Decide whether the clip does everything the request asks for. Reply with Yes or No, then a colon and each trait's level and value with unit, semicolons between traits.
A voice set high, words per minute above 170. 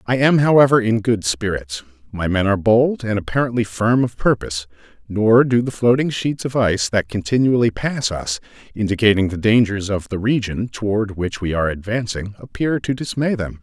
No: low, 110 Hz; average, 180 wpm